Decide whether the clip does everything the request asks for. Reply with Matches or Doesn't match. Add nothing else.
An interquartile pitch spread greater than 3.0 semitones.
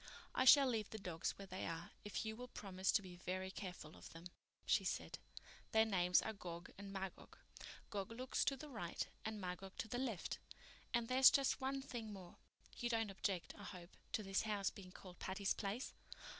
Matches